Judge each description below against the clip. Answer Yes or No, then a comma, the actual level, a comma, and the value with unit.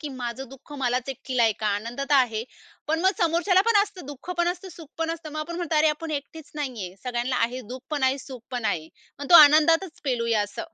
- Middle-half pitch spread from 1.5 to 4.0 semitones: No, average, 4.8 semitones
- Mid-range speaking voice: No, very high, 280 Hz